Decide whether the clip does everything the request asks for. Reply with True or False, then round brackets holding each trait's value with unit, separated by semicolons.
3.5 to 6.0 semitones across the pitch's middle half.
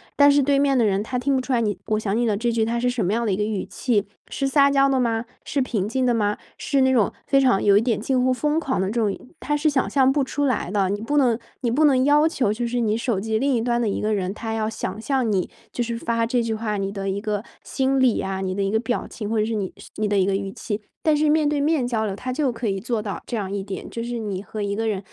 True (4.1 semitones)